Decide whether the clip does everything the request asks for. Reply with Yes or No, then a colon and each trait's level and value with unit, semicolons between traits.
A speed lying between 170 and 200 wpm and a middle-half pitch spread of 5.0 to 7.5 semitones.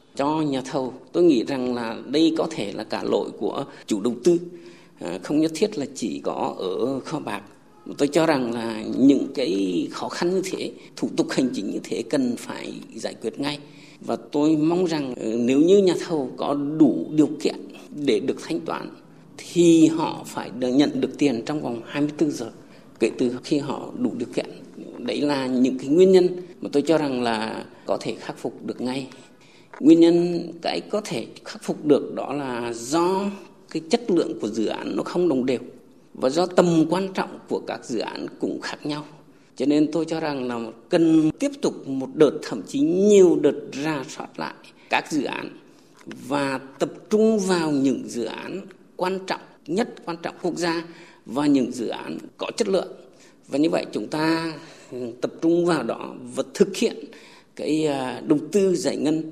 Yes: average, 190 wpm; average, 5.3 semitones